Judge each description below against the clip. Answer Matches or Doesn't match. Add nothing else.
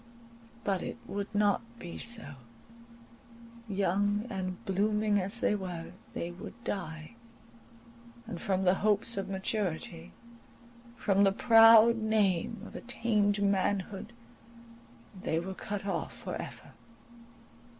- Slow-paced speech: Matches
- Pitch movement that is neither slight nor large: Doesn't match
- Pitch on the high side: Matches